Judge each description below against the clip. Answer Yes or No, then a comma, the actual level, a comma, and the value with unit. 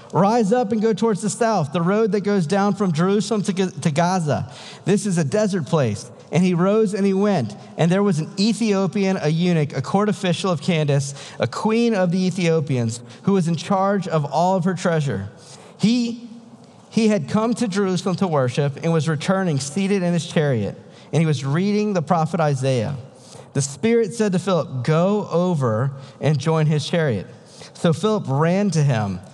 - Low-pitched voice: No, medium, 180 Hz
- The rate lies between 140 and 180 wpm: No, average, 190 wpm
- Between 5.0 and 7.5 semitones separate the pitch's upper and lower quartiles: Yes, average, 5.3 semitones